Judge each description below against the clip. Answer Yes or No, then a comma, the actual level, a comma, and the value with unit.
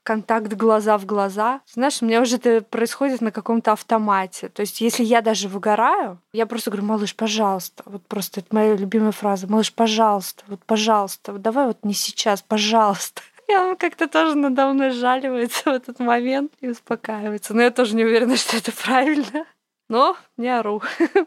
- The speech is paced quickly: Yes, fast, 180 wpm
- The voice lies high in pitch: Yes, high, 230 Hz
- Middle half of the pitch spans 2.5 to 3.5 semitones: Yes, average, 3.1 semitones